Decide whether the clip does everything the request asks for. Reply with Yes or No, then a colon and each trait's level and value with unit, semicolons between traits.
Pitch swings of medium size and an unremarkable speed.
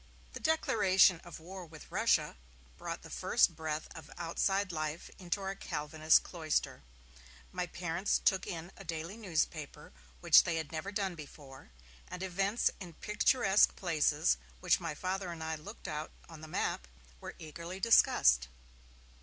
Yes: average, 3.5 semitones; average, 150 wpm